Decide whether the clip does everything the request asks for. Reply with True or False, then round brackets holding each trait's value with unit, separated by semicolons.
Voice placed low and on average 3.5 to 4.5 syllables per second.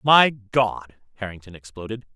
True (110 Hz; 4.4 syllables/s)